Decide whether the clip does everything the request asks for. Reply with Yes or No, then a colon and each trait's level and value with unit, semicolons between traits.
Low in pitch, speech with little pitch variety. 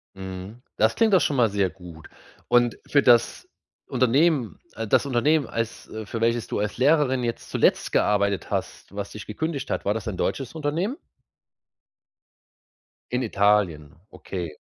No: low, 115 Hz; average, 5.2 semitones